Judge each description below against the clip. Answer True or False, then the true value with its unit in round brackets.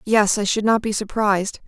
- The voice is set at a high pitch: True (210 Hz)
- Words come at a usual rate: False (215 wpm)